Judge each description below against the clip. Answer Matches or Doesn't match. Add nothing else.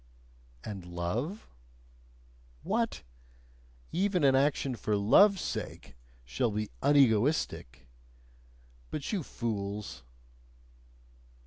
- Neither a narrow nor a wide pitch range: Doesn't match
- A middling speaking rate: Doesn't match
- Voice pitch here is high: Doesn't match